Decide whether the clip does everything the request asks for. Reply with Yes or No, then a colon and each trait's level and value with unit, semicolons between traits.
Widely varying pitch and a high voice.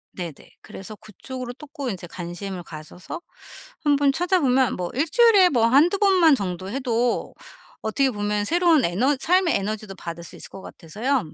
Yes: wide, 7.2 semitones; high, 240 Hz